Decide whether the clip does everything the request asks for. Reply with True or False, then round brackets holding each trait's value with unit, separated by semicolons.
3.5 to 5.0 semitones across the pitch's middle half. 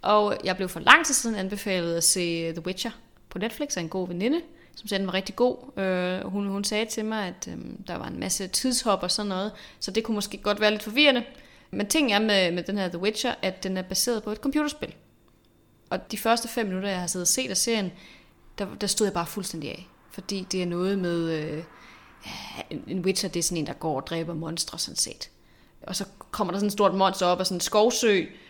False (3.0 semitones)